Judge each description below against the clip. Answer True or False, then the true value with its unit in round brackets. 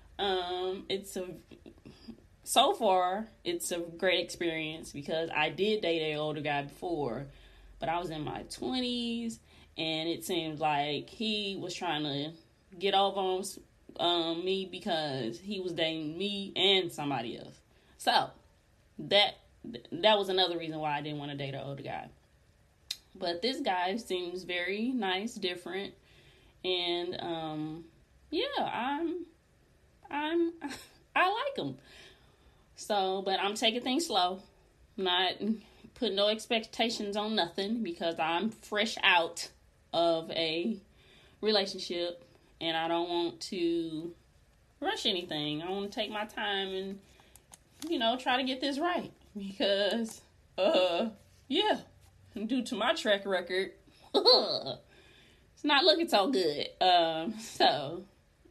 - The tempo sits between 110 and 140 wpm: True (135 wpm)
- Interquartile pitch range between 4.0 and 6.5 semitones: True (4.7 semitones)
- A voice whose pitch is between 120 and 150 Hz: False (190 Hz)